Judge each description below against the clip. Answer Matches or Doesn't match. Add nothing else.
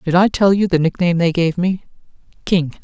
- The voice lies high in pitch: Doesn't match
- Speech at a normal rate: Matches